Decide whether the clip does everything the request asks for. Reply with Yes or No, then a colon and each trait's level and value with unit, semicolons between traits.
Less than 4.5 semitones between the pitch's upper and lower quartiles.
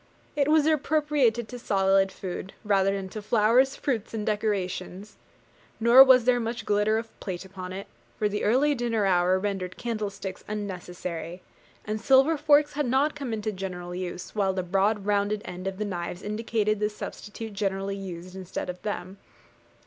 Yes: average, 3.5 semitones